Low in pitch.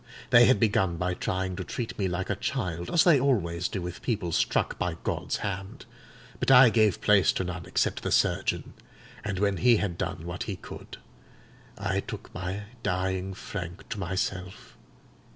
Yes: very low, 95 Hz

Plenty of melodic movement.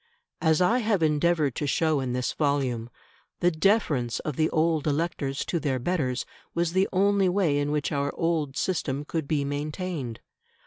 No: average, 3.5 semitones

